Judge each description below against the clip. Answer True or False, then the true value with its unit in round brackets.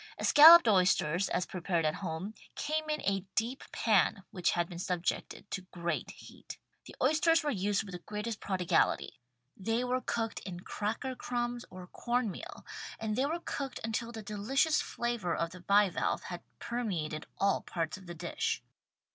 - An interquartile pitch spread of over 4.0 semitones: True (5.3 semitones)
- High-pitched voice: True (205 Hz)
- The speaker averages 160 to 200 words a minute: True (170 wpm)